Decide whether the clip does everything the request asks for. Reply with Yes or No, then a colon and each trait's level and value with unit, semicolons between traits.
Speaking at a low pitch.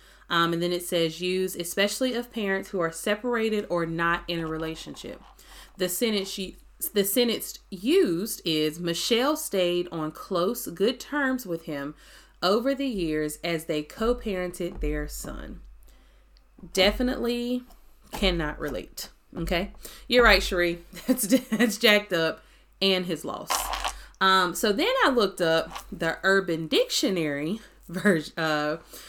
No: medium, 185 Hz